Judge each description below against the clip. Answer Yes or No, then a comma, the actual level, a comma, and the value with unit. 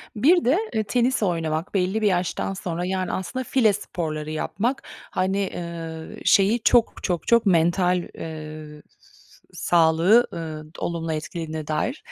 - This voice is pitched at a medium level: Yes, medium, 175 Hz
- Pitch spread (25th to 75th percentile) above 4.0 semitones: Yes, average, 4.6 semitones